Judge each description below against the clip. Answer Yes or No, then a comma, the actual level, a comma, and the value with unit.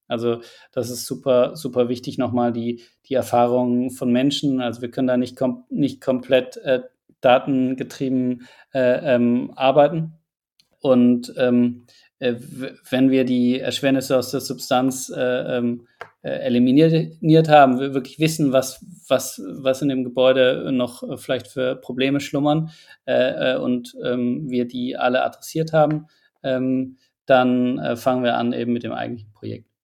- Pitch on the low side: Yes, low, 130 Hz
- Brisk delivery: No, average, 150 wpm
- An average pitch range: No, narrow, 1.8 semitones